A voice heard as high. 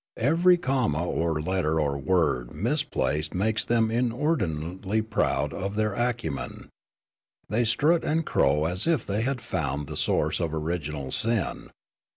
No: low, 100 Hz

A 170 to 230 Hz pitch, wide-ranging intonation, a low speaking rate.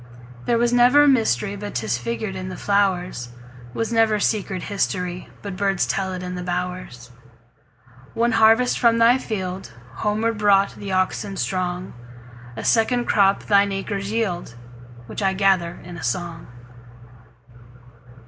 Yes: medium, 185 Hz; wide, 8.9 semitones; slow, 120 wpm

